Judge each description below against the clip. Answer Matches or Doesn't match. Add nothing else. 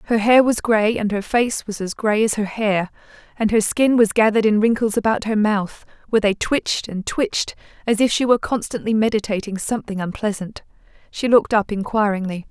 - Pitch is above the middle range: Matches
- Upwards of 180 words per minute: Matches